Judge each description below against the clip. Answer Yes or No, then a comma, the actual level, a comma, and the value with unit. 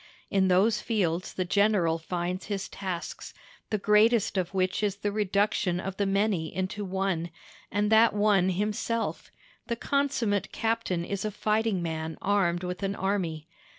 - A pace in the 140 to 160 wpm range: Yes, average, 150 wpm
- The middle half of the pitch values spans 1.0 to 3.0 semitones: Yes, average, 2.7 semitones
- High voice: Yes, high, 195 Hz